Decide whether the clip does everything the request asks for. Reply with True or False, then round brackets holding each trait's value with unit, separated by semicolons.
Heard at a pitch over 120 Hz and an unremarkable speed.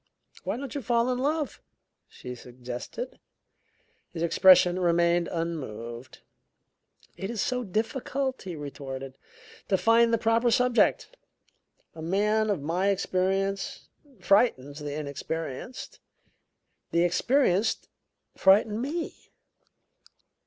False (190 Hz; 105 wpm)